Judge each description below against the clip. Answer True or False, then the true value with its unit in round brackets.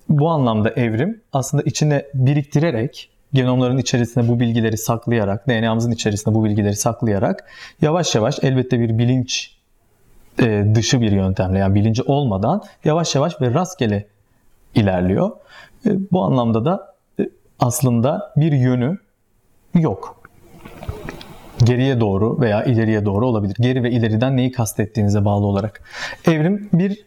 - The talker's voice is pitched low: True (120 Hz)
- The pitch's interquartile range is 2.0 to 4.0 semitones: False (4.5 semitones)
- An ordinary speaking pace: True (120 wpm)